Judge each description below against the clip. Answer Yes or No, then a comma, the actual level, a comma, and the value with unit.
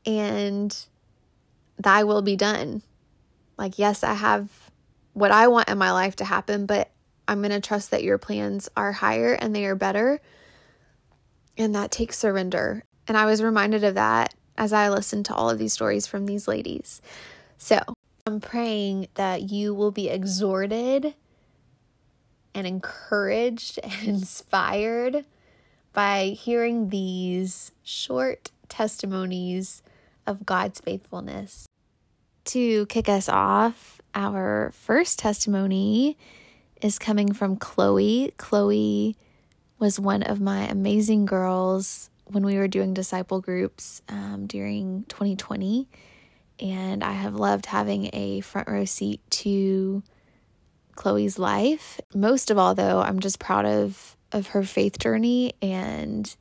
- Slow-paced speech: Yes, slow, 130 wpm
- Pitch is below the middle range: No, high, 195 Hz